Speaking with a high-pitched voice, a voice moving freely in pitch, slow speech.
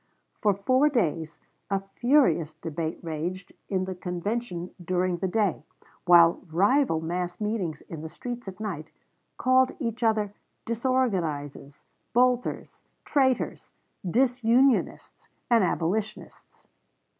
Yes: high, 195 Hz; wide, 6.0 semitones; slow, 110 wpm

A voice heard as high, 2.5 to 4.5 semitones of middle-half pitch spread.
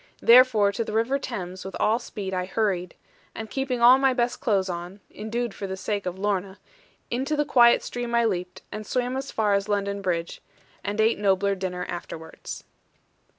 Yes: high, 210 Hz; average, 3.8 semitones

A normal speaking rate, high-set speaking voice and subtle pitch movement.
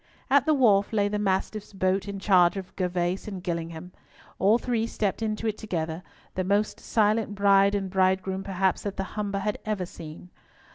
Yes: average, 180 wpm; high, 195 Hz; narrow, 2.2 semitones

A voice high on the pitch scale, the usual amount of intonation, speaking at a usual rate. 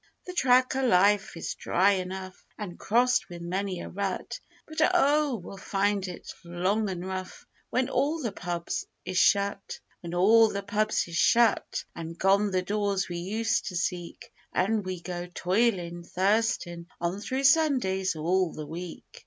Yes: high, 195 Hz; average, 3.9 semitones; average, 160 wpm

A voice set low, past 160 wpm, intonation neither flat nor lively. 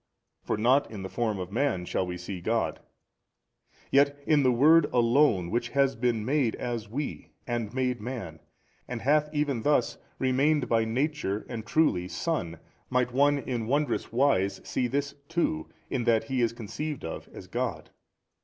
Yes: low, 125 Hz; average, 170 wpm; average, 4.4 semitones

